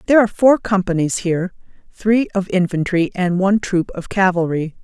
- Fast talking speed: No, average, 150 wpm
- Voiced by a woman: Yes, female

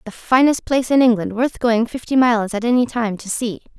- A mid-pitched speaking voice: No, high, 235 Hz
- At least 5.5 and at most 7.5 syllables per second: Yes, 5.7 syllables/s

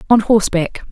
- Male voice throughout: No, female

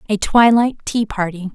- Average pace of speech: Yes, average, 155 wpm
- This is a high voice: Yes, high, 210 Hz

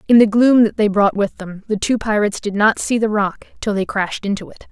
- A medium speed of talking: No, fast, 265 wpm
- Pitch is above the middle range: Yes, high, 210 Hz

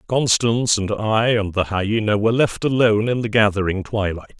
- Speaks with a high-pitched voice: No, low, 110 Hz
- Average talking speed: Yes, average, 180 wpm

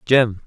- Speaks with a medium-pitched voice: No, low, 115 Hz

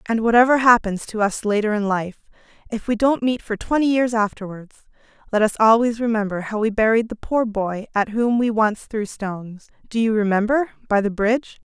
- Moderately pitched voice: No, high, 220 Hz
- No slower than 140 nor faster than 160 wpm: No, average, 195 wpm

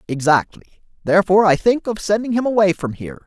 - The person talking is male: Yes, male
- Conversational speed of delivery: Yes, average, 185 wpm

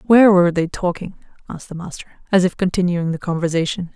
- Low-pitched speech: No, medium, 180 Hz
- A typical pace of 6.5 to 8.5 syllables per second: Yes, 6.9 syllables/s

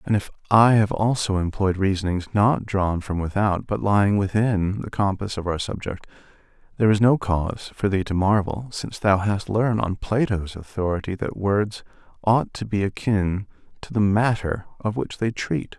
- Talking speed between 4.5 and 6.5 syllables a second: Yes, 4.8 syllables/s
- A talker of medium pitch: No, low, 100 Hz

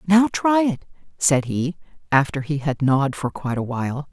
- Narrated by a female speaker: Yes, female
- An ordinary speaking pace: Yes, average, 190 wpm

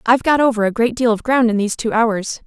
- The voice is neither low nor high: No, high, 230 Hz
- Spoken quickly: Yes, fast, 290 wpm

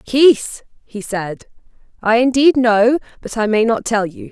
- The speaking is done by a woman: Yes, female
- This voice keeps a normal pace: Yes, average, 165 wpm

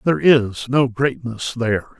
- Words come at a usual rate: Yes, average, 150 wpm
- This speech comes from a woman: No, male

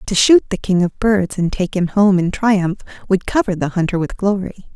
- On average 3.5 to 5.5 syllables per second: Yes, 5.1 syllables/s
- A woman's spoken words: Yes, female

